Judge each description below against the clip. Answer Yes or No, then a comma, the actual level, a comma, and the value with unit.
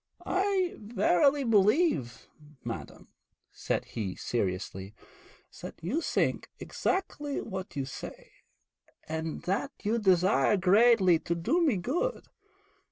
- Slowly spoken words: Yes, slow, 105 wpm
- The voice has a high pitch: Yes, high, 195 Hz